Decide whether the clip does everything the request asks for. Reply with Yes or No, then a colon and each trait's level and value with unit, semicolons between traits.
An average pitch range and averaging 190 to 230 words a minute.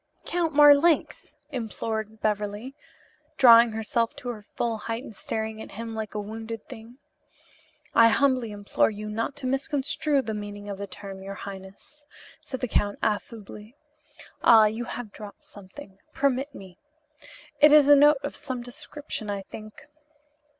No: average, 4.3 semitones; average, 150 wpm